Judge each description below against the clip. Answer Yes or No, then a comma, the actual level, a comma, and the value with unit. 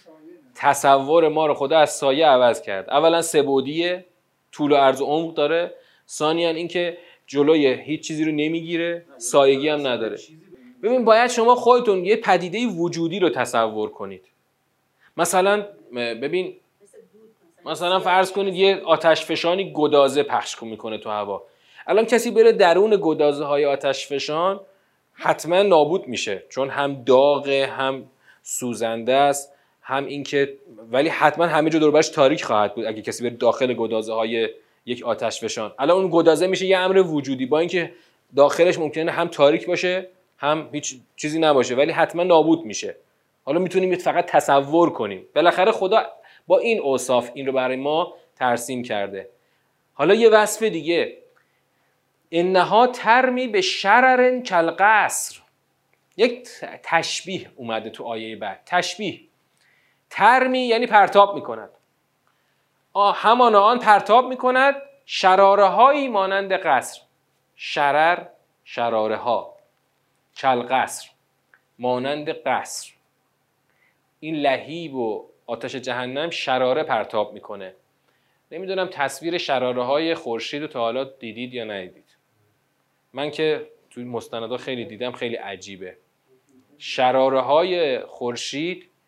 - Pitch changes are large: Yes, wide, 6.2 semitones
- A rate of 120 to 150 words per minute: Yes, average, 130 wpm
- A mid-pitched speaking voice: Yes, medium, 160 Hz